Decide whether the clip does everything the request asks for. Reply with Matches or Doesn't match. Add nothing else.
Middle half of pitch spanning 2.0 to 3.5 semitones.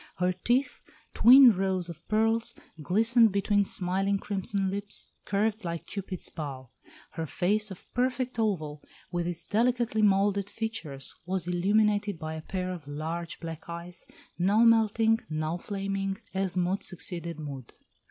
Doesn't match